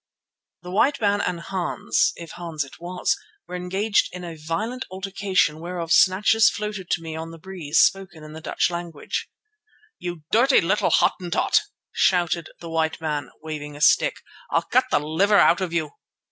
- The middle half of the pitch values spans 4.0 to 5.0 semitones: No, average, 3.2 semitones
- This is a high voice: No, medium, 175 Hz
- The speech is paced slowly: No, average, 165 wpm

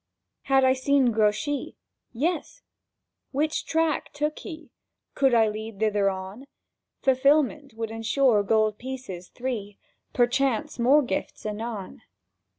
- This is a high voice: Yes, high, 245 Hz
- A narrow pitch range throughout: No, average, 4.6 semitones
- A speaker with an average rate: No, slow, 115 wpm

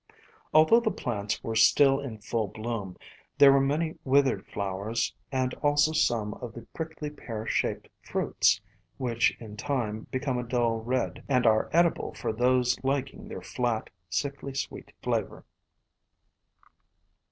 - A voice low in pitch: Yes, low, 125 Hz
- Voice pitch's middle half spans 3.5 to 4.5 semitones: Yes, average, 4.0 semitones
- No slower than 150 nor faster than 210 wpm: No, average, 140 wpm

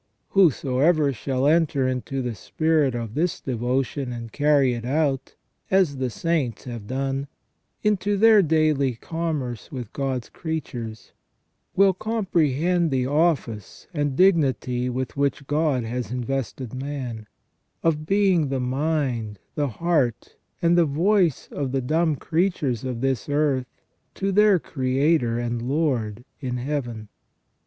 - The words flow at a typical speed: No, slow, 130 wpm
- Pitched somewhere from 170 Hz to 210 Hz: No, low, 135 Hz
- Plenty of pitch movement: No, average, 4.4 semitones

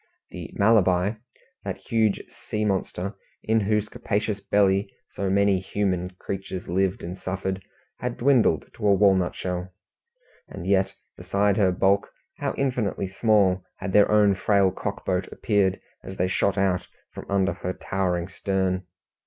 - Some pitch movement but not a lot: No, narrow, 1.7 semitones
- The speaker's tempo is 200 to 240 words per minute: No, average, 145 wpm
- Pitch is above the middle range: No, very low, 95 Hz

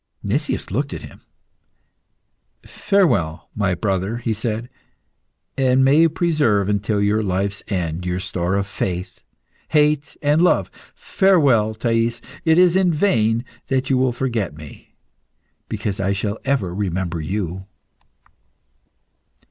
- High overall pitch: No, low, 110 Hz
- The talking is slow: Yes, slow, 125 wpm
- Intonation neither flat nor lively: No, wide, 6.1 semitones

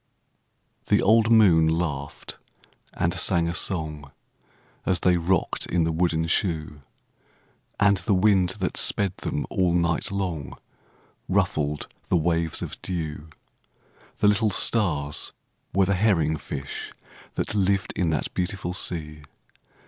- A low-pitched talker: Yes, very low, 85 Hz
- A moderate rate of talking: No, slow, 125 wpm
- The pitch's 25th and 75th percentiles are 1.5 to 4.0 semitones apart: Yes, average, 3.3 semitones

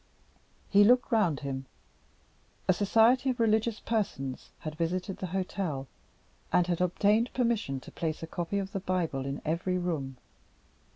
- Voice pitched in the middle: Yes, medium, 180 Hz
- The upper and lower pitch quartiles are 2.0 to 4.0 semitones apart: No, average, 5.2 semitones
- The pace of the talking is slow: No, average, 150 wpm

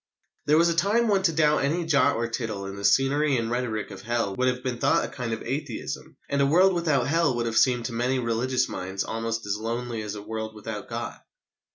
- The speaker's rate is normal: No, fast, 235 wpm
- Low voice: Yes, low, 125 Hz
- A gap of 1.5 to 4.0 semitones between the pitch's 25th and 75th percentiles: No, average, 4.4 semitones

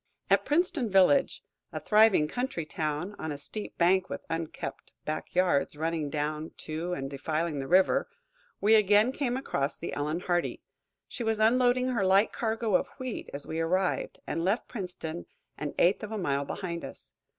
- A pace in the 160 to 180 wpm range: Yes, average, 170 wpm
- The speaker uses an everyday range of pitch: No, wide, 5.9 semitones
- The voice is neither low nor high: Yes, medium, 180 Hz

